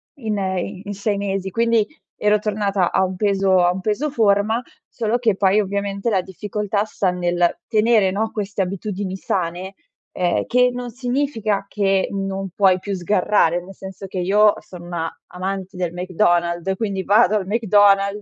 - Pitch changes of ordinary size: No, narrow, 2.2 semitones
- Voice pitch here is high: Yes, high, 195 Hz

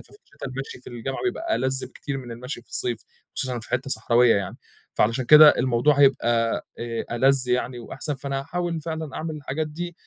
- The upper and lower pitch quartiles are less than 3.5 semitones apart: No, average, 3.9 semitones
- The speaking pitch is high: No, low, 135 Hz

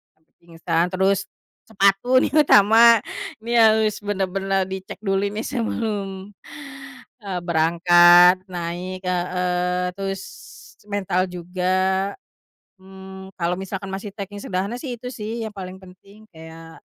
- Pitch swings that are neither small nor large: No, narrow, 2.2 semitones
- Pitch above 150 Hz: Yes, high, 190 Hz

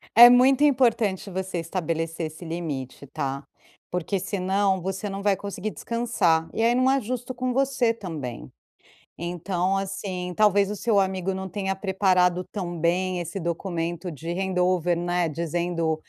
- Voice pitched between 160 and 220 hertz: Yes, medium, 185 Hz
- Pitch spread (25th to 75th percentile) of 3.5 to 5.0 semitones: No, average, 3.1 semitones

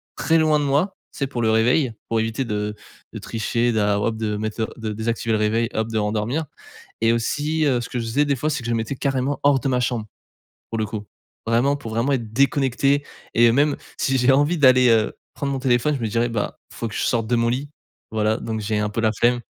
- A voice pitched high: No, low, 120 Hz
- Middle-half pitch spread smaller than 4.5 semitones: Yes, average, 3.7 semitones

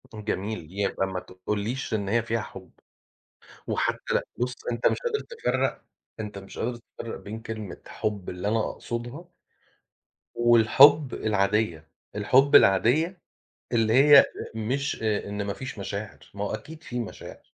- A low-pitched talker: Yes, low, 110 Hz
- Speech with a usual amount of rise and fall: Yes, average, 3.5 semitones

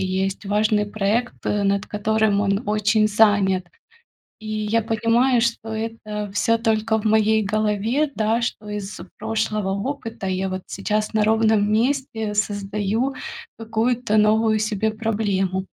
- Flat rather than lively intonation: Yes, narrow, 1.4 semitones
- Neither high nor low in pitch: No, high, 215 Hz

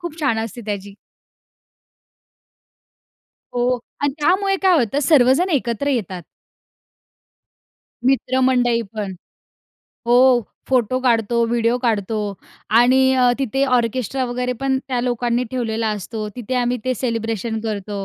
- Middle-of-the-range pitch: No, high, 245 Hz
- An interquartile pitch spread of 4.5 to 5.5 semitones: No, narrow, 2.6 semitones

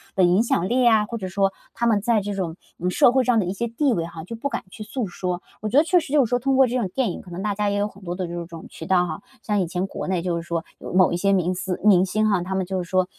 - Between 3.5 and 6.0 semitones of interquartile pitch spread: Yes, average, 4.2 semitones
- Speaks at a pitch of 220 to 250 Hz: No, high, 195 Hz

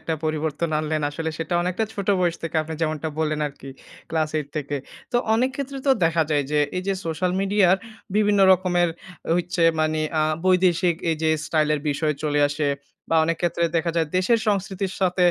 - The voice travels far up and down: No, average, 3.0 semitones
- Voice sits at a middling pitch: Yes, medium, 165 Hz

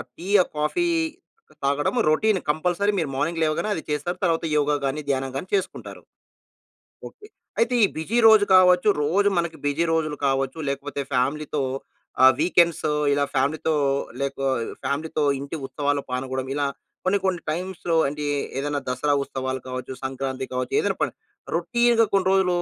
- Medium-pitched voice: Yes, medium, 150 Hz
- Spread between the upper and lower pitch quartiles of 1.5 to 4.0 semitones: No, average, 4.6 semitones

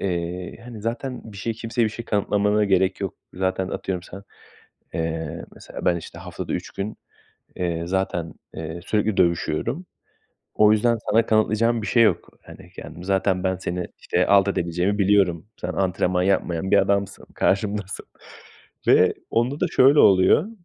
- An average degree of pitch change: Yes, average, 3.1 semitones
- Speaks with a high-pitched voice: No, very low, 95 Hz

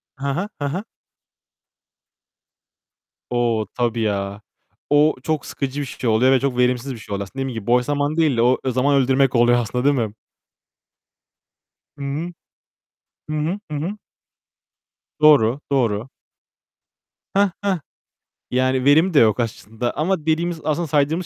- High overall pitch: No, low, 135 Hz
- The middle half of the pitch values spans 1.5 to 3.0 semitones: No, average, 4.0 semitones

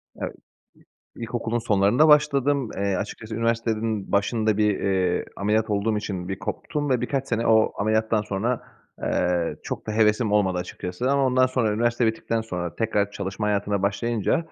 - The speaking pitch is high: No, low, 110 Hz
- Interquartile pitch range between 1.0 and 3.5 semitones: Yes, average, 2.8 semitones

